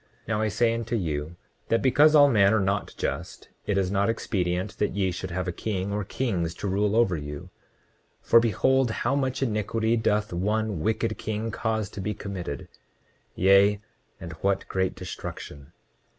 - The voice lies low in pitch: Yes, low, 105 Hz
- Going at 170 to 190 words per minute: Yes, average, 180 wpm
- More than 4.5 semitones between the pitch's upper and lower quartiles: No, average, 3.3 semitones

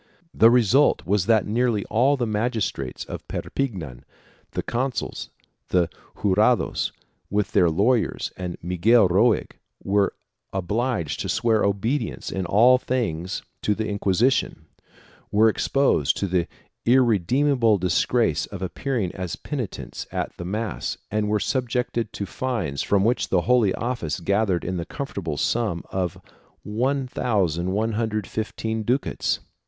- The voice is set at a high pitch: No, low, 105 Hz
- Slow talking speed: Yes, slow, 130 wpm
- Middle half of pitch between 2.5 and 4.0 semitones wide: No, average, 4.6 semitones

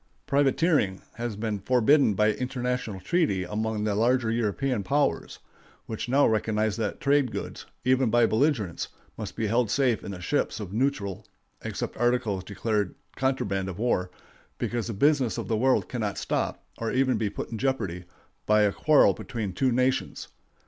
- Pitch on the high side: No, low, 115 Hz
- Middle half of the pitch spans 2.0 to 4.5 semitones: Yes, average, 4.0 semitones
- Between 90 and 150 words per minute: No, average, 165 wpm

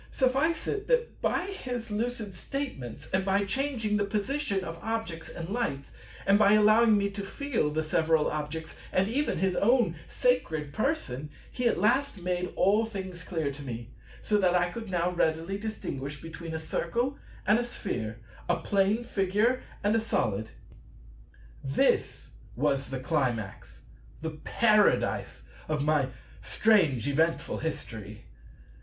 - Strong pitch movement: Yes, wide, 6.5 semitones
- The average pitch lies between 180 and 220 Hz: Yes, high, 190 Hz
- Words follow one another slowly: No, average, 145 wpm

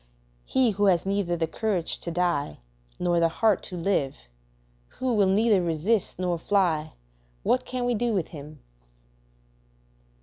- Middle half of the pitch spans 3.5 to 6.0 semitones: Yes, average, 4.0 semitones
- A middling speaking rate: Yes, average, 145 wpm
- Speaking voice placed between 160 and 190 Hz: Yes, medium, 185 Hz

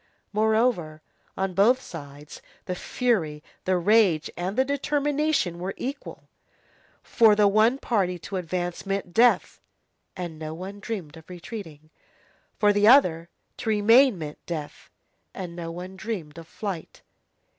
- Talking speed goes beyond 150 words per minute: No, slow, 135 wpm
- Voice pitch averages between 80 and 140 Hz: No, high, 190 Hz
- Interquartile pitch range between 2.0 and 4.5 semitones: No, average, 5.0 semitones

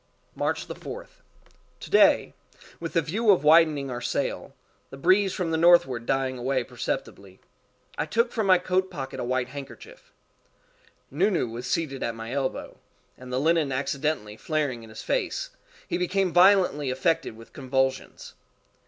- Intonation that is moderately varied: No, wide, 5.8 semitones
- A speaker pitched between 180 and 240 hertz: No, medium, 145 Hz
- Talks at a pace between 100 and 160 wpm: Yes, average, 155 wpm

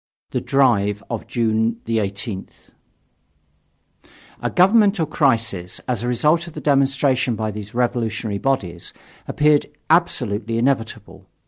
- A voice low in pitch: Yes, low, 120 Hz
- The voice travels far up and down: No, average, 4.5 semitones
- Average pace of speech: No, slow, 110 wpm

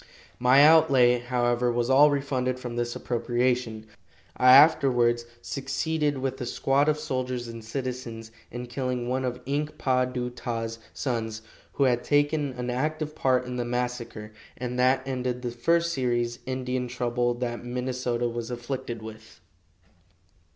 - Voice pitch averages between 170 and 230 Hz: No, low, 125 Hz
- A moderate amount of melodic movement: No, narrow, 1.7 semitones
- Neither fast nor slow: Yes, average, 145 wpm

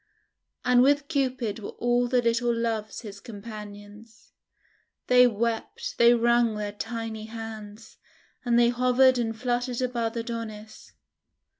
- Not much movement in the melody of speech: Yes, narrow, 2.0 semitones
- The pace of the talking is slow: Yes, slow, 125 wpm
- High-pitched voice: Yes, high, 230 Hz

